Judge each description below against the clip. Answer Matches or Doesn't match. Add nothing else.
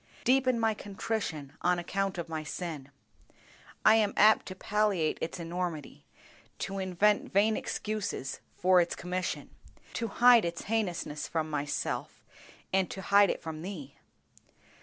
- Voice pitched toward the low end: Doesn't match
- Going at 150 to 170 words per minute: Doesn't match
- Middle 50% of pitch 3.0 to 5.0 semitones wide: Matches